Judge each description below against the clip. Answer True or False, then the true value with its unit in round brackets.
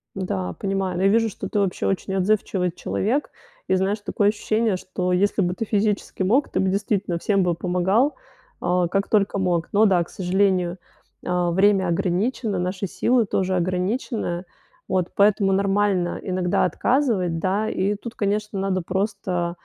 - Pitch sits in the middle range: False (195 Hz)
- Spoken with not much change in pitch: True (2.3 semitones)